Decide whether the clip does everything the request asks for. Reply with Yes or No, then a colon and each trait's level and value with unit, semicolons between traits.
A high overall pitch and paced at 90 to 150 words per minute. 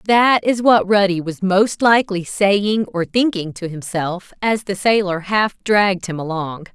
No: high, 195 Hz; average, 170 wpm